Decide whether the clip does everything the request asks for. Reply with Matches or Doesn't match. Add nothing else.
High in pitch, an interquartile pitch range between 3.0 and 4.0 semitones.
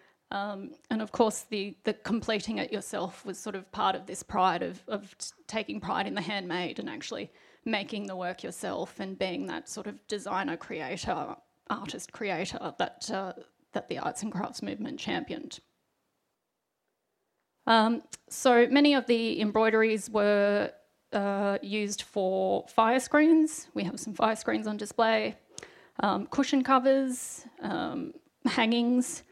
Matches